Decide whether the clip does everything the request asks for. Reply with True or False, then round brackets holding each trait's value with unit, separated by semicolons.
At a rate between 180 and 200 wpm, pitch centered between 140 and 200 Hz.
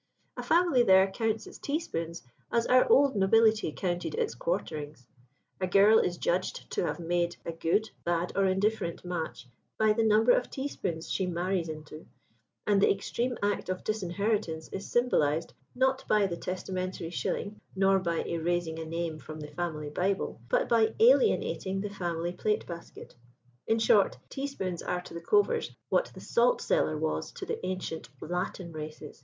False (165 wpm; 185 Hz)